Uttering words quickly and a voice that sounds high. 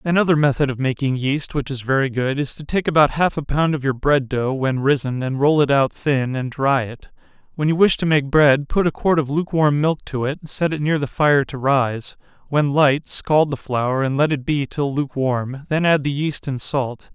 No: fast, 230 wpm; medium, 140 Hz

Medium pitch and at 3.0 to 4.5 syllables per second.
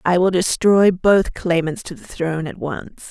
Yes: medium, 180 Hz; 4.4 syllables/s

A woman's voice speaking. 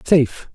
No: male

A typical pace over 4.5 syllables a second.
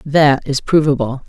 No: 4.3 syllables/s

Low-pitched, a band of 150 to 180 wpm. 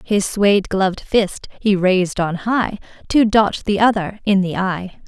No: high, 200 Hz; average, 175 wpm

